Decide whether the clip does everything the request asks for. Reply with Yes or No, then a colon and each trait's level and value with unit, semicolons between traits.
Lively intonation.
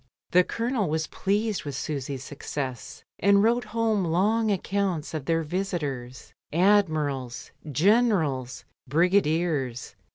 Yes: wide, 6.0 semitones